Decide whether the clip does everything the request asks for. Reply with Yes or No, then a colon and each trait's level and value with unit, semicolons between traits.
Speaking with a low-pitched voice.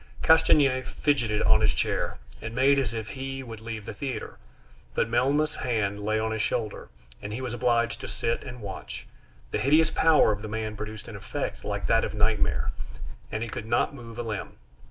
Yes: low, 115 Hz